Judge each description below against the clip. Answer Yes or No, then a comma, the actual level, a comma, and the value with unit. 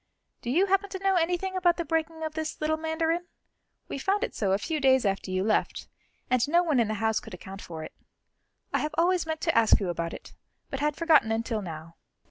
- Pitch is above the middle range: Yes, very high, 305 Hz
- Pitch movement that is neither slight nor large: No, wide, 7.6 semitones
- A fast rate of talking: Yes, fast, 230 wpm